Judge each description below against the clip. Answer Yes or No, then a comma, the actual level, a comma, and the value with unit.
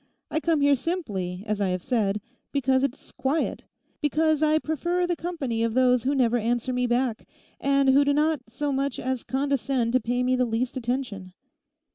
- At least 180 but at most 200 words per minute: Yes, average, 185 wpm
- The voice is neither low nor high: No, very high, 260 Hz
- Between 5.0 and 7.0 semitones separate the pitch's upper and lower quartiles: No, average, 3.4 semitones